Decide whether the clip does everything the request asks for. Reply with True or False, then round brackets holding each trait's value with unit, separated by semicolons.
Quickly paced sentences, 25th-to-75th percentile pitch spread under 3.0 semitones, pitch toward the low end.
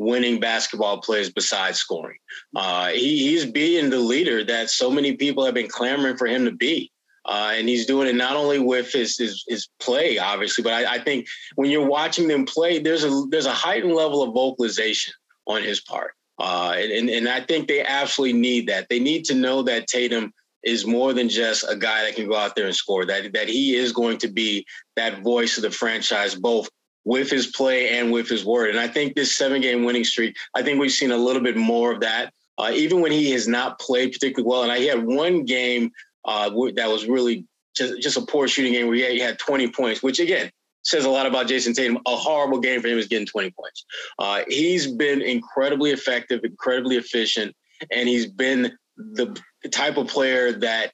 True (220 wpm; 2.6 semitones; 125 Hz)